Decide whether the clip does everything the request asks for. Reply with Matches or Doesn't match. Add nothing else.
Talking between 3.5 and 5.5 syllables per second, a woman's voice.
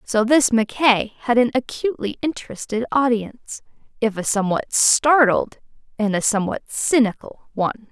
Matches